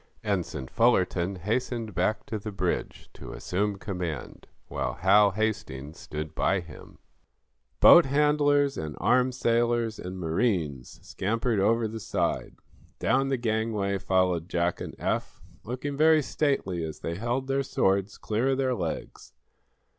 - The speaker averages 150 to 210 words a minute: No, average, 140 wpm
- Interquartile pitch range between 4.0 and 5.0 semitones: No, wide, 5.4 semitones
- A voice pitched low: Yes, low, 105 Hz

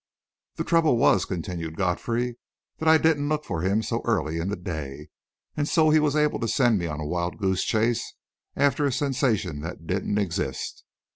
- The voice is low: Yes, low, 105 Hz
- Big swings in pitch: Yes, wide, 8.7 semitones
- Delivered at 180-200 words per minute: Yes, average, 190 wpm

